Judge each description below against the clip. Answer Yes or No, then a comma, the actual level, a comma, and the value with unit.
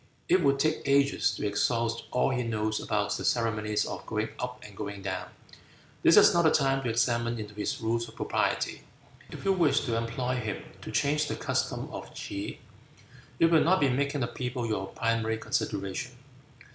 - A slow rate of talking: No, average, 185 wpm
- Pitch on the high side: No, low, 115 Hz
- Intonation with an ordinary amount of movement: Yes, average, 4.2 semitones